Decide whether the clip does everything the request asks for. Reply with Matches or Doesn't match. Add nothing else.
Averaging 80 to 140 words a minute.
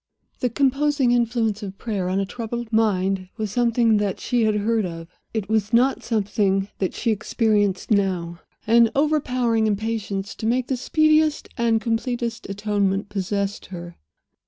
Doesn't match